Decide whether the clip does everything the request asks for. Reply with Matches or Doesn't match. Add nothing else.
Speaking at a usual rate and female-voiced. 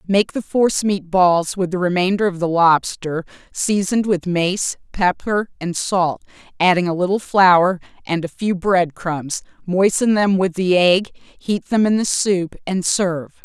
Matches